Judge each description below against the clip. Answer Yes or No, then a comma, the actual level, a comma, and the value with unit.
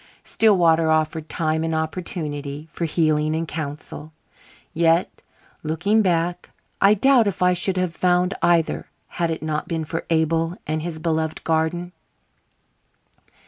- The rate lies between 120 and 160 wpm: Yes, slow, 135 wpm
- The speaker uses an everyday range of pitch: No, narrow, 2.0 semitones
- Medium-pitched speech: Yes, medium, 165 Hz